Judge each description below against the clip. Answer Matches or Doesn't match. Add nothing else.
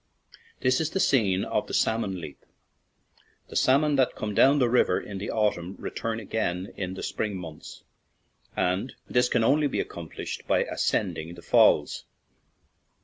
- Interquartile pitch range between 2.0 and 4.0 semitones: Doesn't match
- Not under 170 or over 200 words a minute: Doesn't match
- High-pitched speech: Doesn't match